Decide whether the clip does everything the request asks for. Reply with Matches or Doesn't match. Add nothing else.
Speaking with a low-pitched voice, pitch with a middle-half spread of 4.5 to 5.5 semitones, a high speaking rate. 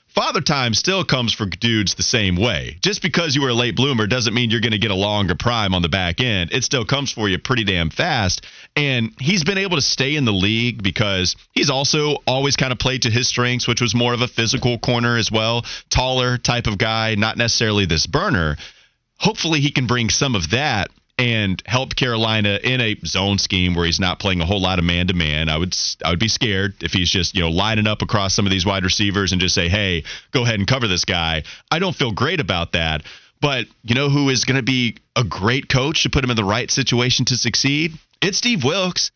Matches